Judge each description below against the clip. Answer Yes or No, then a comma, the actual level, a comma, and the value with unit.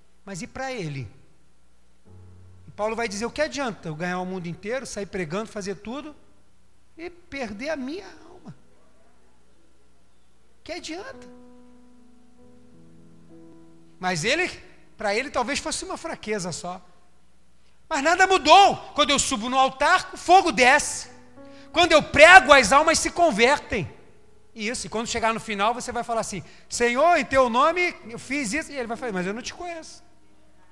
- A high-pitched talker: Yes, high, 245 Hz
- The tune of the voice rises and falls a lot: Yes, wide, 8.4 semitones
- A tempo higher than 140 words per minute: Yes, average, 160 wpm